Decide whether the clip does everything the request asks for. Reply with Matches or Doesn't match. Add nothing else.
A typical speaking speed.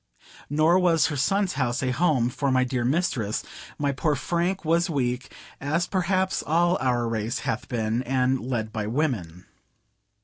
Matches